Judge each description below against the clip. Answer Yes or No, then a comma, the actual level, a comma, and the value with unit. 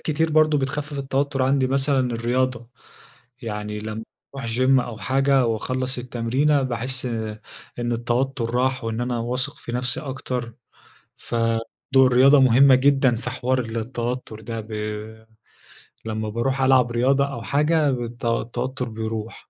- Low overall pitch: Yes, low, 125 Hz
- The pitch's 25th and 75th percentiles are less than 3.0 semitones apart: Yes, narrow, 2.5 semitones